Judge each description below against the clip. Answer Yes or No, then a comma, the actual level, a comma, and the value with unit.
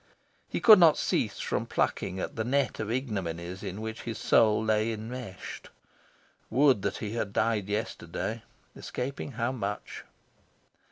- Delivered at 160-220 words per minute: No, average, 145 wpm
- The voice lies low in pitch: Yes, low, 110 Hz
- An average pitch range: Yes, average, 3.4 semitones